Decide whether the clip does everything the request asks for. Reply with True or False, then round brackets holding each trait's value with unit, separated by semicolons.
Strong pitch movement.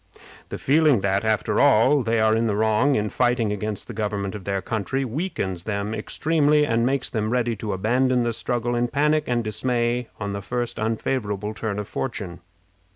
False (3.3 semitones)